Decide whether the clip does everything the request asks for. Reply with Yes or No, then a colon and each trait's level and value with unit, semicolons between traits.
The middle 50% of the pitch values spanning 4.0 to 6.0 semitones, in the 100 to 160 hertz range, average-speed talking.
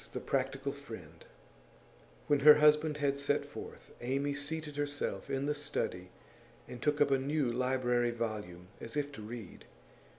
No: average, 3.5 semitones; low, 135 Hz; average, 155 wpm